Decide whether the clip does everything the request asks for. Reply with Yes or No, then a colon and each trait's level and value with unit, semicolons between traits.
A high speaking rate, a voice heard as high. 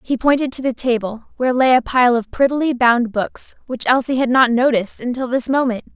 Yes: fast, 210 wpm; very high, 250 Hz